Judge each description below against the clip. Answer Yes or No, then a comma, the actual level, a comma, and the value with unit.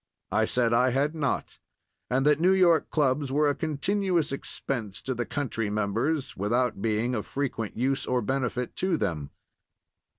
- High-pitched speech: No, low, 130 Hz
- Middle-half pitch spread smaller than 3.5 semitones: No, average, 4.5 semitones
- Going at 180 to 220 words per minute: No, average, 160 wpm